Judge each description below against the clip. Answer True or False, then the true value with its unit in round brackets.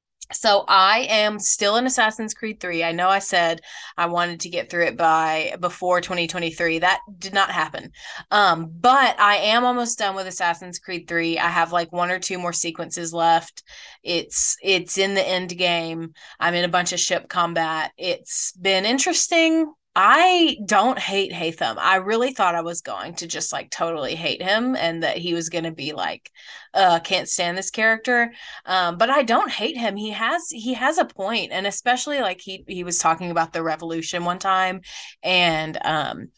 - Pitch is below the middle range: False (185 Hz)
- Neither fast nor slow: True (190 wpm)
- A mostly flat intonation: False (4.0 semitones)